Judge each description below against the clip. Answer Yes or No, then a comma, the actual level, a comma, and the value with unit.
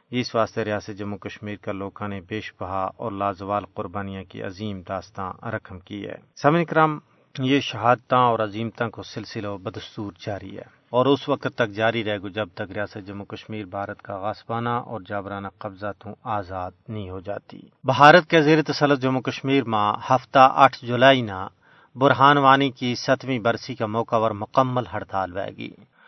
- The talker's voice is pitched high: No, low, 110 Hz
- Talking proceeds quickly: No, average, 170 wpm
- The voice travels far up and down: No, average, 4.3 semitones